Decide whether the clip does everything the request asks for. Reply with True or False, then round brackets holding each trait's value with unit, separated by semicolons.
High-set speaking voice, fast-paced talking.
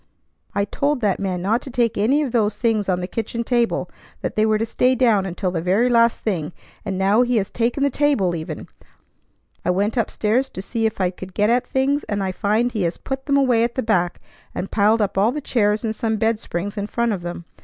True (220 Hz; 240 wpm)